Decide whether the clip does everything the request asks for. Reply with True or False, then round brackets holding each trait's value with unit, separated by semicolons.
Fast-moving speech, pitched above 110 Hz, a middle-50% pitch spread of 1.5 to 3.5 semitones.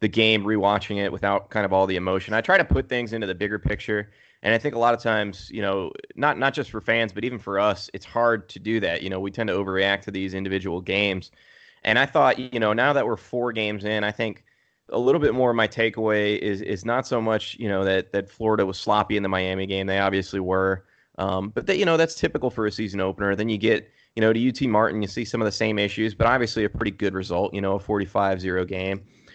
False (265 wpm; 105 Hz; 2.6 semitones)